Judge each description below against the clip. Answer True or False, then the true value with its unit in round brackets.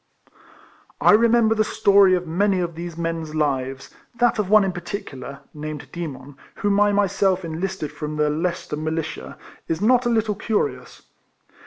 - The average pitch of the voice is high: False (175 Hz)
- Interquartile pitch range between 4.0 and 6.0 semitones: True (5.1 semitones)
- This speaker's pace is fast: False (155 wpm)